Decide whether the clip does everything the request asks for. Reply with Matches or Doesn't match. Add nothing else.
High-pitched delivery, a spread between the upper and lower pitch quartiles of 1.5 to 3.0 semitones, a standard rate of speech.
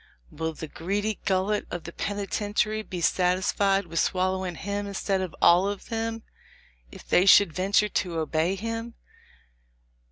Matches